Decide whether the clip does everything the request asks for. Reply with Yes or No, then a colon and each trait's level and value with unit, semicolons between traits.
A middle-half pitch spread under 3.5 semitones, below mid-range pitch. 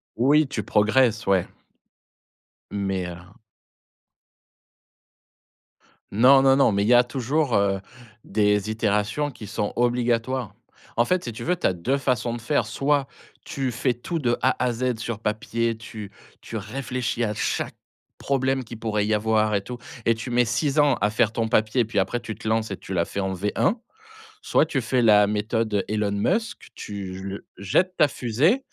No: average, 3.8 semitones; low, 115 Hz